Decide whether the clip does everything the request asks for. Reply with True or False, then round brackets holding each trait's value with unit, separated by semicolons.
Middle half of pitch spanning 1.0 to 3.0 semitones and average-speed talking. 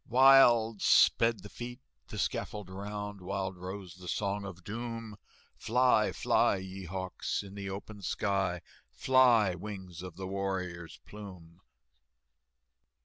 False (2.7 semitones; 125 wpm)